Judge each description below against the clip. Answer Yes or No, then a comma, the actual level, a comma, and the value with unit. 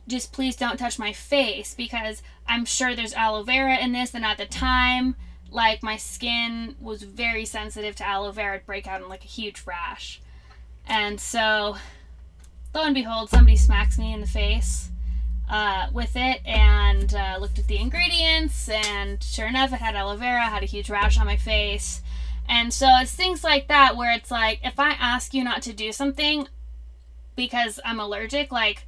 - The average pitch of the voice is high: Yes, high, 220 Hz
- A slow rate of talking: No, average, 185 wpm